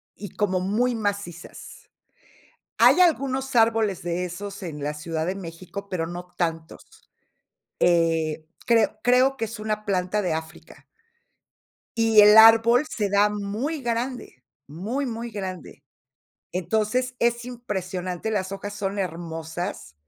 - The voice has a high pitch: Yes, high, 205 Hz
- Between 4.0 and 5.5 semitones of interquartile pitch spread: Yes, average, 4.6 semitones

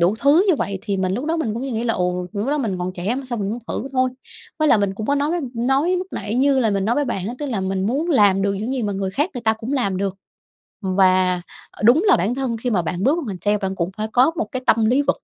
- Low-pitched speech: No, high, 225 Hz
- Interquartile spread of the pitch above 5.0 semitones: Yes, wide, 5.6 semitones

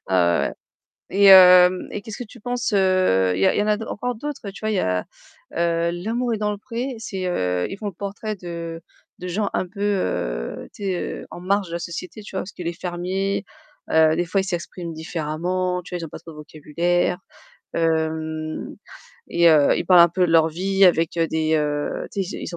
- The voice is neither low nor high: Yes, medium, 180 Hz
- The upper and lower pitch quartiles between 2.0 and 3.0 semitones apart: No, average, 3.5 semitones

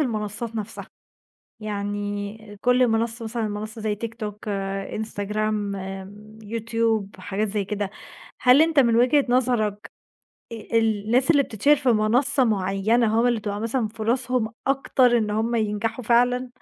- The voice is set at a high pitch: Yes, high, 220 Hz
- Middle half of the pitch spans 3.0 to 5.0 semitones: No, narrow, 2.6 semitones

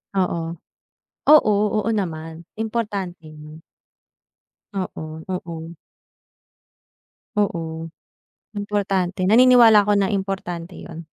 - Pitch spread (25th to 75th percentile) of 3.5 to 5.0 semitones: Yes, average, 3.9 semitones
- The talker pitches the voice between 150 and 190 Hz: Yes, medium, 185 Hz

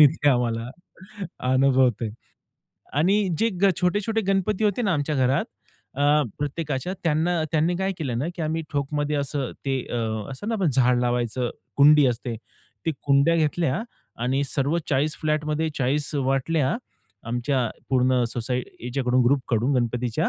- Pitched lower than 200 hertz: Yes, medium, 140 Hz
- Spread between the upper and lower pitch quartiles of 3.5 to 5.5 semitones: Yes, average, 4.0 semitones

